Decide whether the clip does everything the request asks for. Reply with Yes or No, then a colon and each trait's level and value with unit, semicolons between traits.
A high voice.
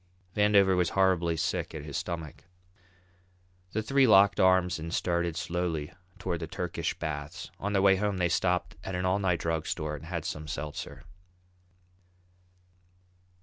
No: very low, 85 Hz